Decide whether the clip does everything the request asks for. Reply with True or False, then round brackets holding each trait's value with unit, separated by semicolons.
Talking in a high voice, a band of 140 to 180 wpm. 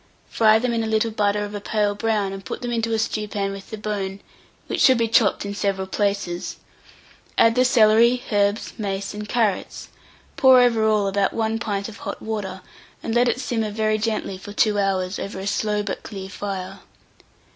False (210 Hz; 195 wpm)